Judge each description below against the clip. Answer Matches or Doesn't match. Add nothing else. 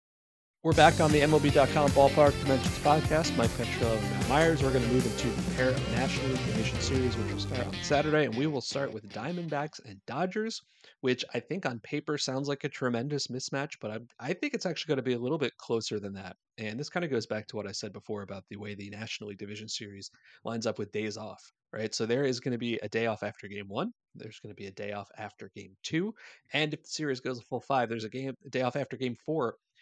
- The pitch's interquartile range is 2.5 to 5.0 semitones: Doesn't match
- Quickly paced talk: Matches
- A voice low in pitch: Matches